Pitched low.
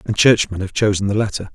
Yes: low, 100 Hz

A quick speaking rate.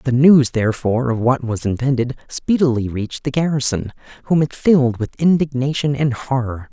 No: average, 160 wpm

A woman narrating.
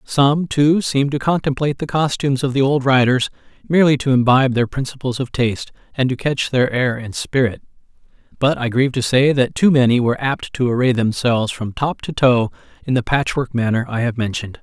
No: male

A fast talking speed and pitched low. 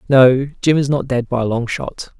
Yes: fast, 245 wpm; low, 130 Hz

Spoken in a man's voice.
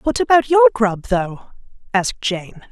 No: female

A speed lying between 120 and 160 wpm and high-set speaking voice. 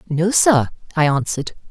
No: average, 140 wpm; medium, 165 Hz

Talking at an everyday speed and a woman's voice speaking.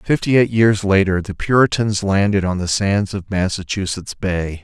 No: average, 170 wpm; male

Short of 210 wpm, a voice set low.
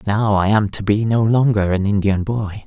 No: fast, 225 wpm; low, 105 Hz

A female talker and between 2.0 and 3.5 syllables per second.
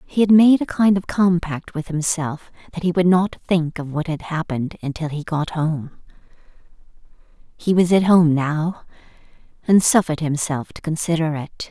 No: female; 4.9 syllables/s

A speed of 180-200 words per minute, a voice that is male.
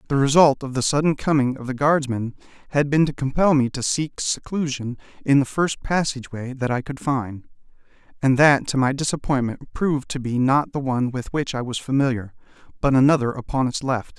Yes: average, 195 wpm; male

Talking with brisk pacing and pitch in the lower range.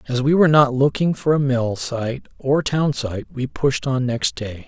Yes: fast, 220 wpm; low, 130 Hz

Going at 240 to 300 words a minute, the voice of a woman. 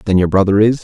No: fast, 285 wpm; male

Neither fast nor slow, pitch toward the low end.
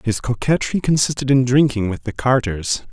Yes: average, 165 wpm; low, 125 Hz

